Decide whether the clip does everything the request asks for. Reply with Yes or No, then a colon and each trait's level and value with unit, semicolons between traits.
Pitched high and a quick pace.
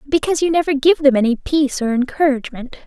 No: very high, 280 Hz; average, 190 wpm